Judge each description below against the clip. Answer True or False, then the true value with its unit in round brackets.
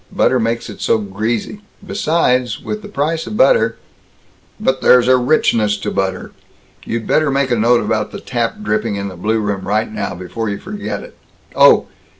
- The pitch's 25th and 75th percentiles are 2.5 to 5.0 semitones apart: True (4.2 semitones)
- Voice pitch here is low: True (115 Hz)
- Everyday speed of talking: True (185 wpm)